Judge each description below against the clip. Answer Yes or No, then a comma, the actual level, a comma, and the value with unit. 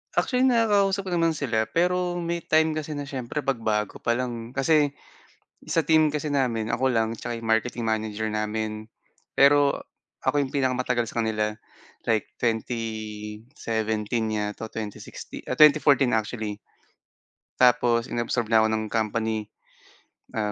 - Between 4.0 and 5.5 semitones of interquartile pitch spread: Yes, average, 4.7 semitones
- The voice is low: Yes, low, 120 Hz